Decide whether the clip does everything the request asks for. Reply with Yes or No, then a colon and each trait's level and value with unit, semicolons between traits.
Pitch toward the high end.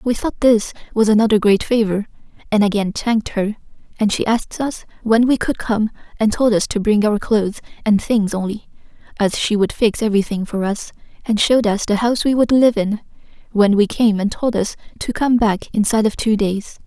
Yes: high, 215 Hz